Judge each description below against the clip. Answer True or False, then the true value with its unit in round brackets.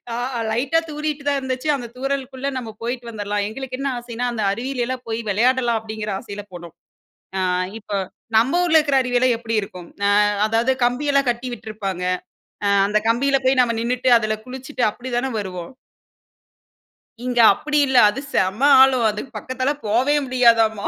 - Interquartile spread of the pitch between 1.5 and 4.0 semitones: True (3.3 semitones)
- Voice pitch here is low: False (245 Hz)